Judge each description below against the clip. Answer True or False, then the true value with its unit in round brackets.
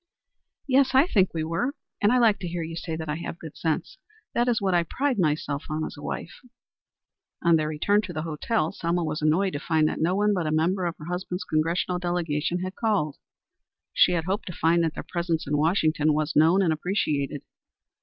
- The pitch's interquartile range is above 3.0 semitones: True (3.5 semitones)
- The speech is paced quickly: True (215 wpm)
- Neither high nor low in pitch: True (170 Hz)